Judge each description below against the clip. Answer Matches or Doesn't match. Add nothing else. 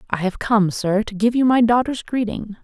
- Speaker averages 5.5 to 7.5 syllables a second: Doesn't match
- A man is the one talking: Doesn't match